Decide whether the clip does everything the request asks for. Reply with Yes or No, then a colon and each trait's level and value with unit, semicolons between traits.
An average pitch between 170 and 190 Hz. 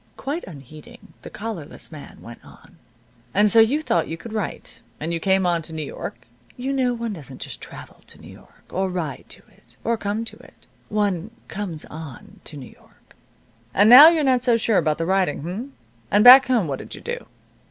No: high, 200 Hz